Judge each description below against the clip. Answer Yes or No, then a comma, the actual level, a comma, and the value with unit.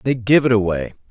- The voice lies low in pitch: Yes, low, 115 Hz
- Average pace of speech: No, fast, 215 wpm